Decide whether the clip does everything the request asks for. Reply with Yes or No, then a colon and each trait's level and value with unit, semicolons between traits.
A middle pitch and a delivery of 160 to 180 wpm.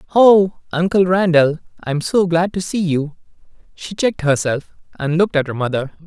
Yes: medium, 170 Hz; average, 170 wpm